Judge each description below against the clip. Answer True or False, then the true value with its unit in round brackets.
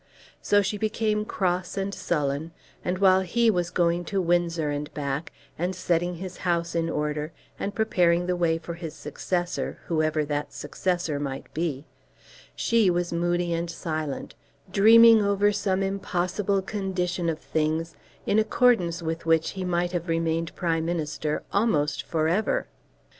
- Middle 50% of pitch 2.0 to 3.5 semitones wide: True (2.8 semitones)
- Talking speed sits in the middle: True (150 wpm)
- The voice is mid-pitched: True (175 Hz)